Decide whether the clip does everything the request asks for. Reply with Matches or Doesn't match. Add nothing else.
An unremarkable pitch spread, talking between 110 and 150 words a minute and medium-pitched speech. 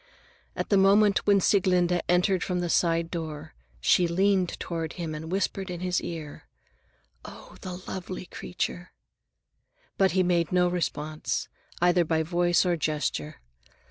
Doesn't match